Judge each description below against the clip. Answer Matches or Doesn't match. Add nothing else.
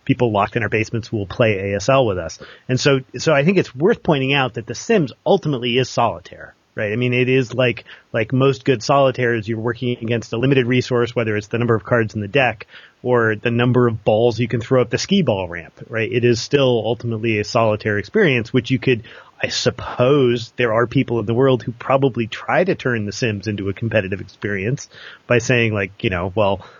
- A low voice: Matches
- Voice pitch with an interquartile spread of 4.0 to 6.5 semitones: Doesn't match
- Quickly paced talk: Matches